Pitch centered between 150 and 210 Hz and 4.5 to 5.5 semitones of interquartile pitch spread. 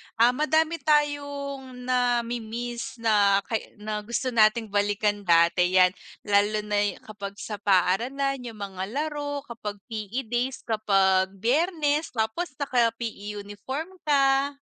No: high, 230 Hz; average, 5.0 semitones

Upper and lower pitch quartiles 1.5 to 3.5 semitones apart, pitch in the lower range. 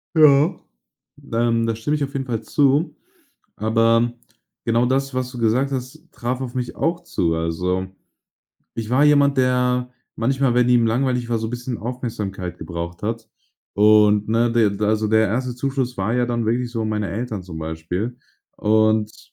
Yes: average, 2.9 semitones; low, 115 Hz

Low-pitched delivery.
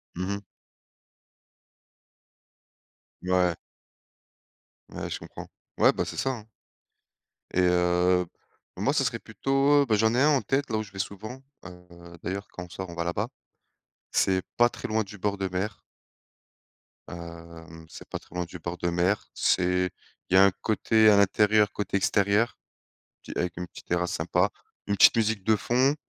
Yes: low, 100 Hz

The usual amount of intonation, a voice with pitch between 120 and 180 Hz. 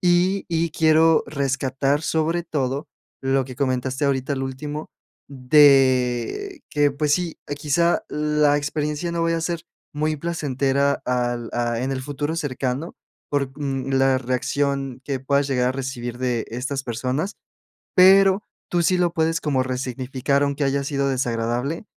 Yes: average, 3.2 semitones; medium, 140 Hz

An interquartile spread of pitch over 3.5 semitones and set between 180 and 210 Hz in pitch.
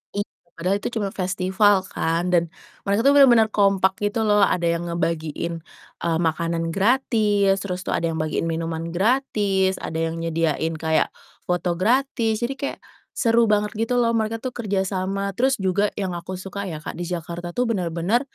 Yes: average, 4.2 semitones; high, 190 Hz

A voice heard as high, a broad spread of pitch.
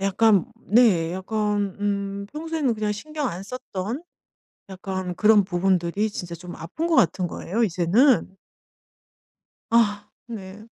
No: high, 205 Hz; average, 3.4 semitones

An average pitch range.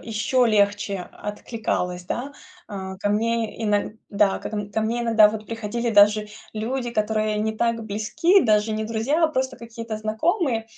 No: narrow, 1.8 semitones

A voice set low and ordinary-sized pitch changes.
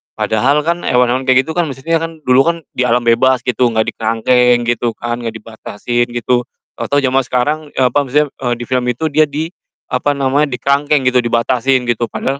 Yes: low, 125 Hz; average, 3.0 semitones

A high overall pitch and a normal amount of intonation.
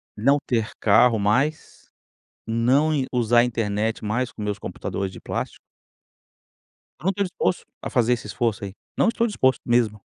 No: low, 120 Hz; average, 3.6 semitones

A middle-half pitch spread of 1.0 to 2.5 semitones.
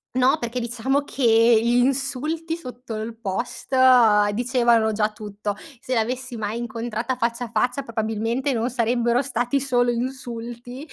Yes: narrow, 2.1 semitones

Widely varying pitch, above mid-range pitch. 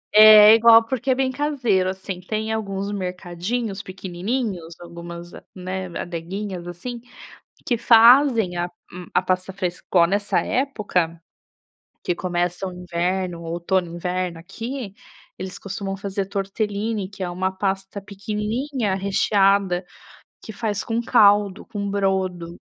No: average, 3.2 semitones; high, 195 Hz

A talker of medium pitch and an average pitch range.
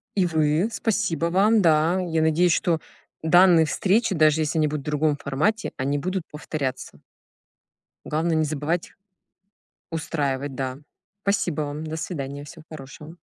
Yes: medium, 160 Hz; average, 3.0 semitones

